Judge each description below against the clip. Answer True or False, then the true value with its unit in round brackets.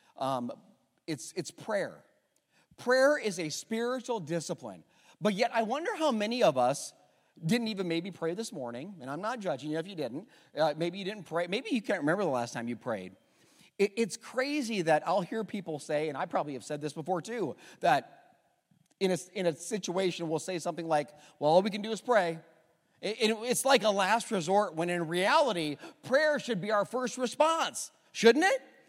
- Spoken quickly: True (210 wpm)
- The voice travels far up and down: True (6.0 semitones)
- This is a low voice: False (195 Hz)